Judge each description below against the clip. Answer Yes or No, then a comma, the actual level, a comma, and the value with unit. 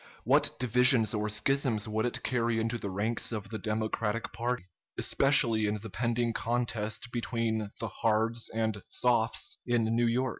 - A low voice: Yes, low, 115 Hz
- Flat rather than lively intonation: Yes, narrow, 1.7 semitones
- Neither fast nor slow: Yes, average, 155 wpm